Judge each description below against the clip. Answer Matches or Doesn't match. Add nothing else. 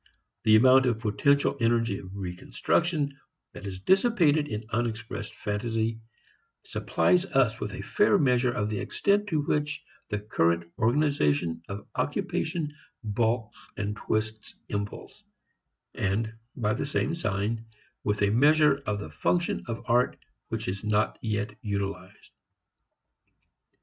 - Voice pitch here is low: Matches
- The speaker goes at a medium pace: Doesn't match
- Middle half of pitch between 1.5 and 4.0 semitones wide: Doesn't match